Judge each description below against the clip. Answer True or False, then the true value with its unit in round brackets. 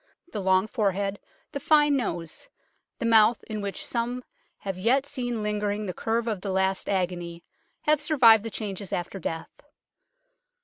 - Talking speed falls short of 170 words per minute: True (150 wpm)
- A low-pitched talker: False (210 Hz)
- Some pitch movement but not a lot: True (3.7 semitones)